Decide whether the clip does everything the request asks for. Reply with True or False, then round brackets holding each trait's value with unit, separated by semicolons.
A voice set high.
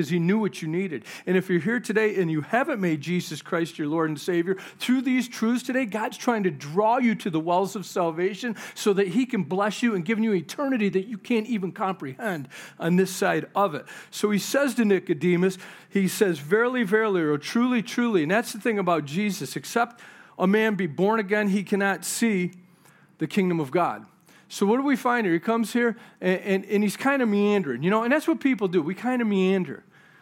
True (200 Hz)